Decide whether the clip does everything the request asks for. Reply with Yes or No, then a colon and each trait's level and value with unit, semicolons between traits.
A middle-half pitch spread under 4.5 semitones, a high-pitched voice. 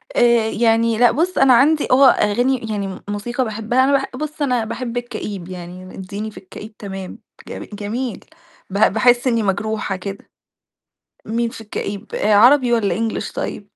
Yes: average, 3.3 semitones; high, 225 Hz